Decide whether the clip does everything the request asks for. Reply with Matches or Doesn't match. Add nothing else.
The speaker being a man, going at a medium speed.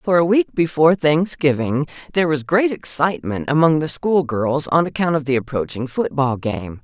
Doesn't match